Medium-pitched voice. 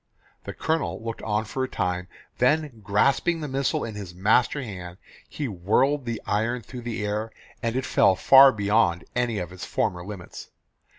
No: low, 110 Hz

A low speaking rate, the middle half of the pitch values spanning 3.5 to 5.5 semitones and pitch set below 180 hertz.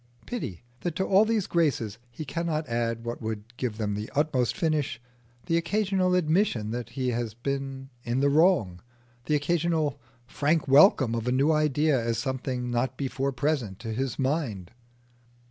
No: average, 165 wpm; average, 5.0 semitones; low, 135 Hz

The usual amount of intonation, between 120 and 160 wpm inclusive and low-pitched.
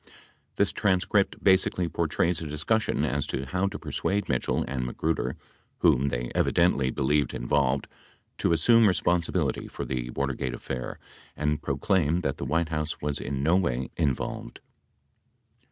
Yes: average, 4.6 semitones; average, 150 wpm; very low, 75 Hz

